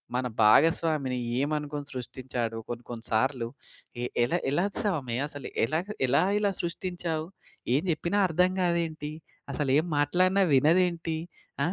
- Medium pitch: Yes, medium, 150 Hz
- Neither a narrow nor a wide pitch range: Yes, average, 4.7 semitones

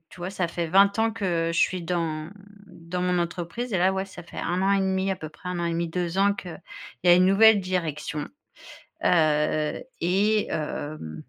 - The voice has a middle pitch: Yes, medium, 180 Hz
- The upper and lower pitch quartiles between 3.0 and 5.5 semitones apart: No, narrow, 2.5 semitones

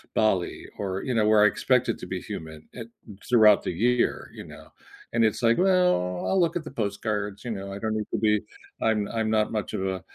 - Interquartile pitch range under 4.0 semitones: Yes, average, 2.8 semitones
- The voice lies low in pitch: Yes, low, 110 Hz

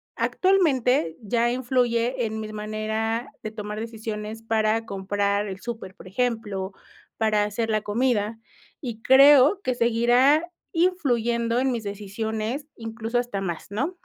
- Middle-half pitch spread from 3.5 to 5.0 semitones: No, average, 2.7 semitones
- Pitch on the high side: Yes, high, 225 Hz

